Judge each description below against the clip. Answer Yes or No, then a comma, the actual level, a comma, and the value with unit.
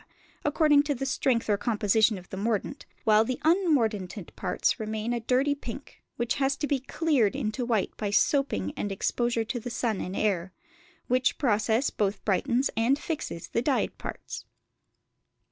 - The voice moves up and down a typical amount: Yes, average, 4.5 semitones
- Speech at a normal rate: Yes, average, 160 wpm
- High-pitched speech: Yes, high, 235 Hz